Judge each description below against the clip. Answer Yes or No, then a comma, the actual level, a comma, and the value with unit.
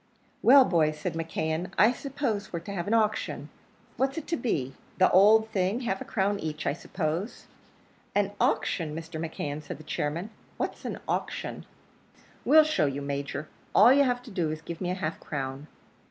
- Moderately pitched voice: Yes, medium, 180 Hz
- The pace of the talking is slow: No, average, 185 wpm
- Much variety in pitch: Yes, wide, 6.1 semitones